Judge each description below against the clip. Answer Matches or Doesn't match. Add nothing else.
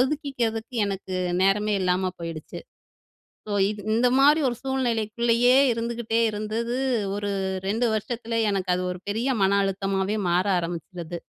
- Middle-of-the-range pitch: Doesn't match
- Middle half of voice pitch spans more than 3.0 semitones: Matches